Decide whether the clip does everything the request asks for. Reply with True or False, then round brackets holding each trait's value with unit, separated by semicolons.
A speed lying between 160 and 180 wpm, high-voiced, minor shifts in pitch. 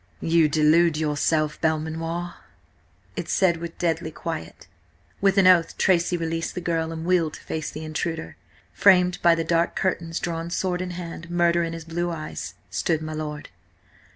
False (165 wpm; 165 Hz; 1.5 semitones)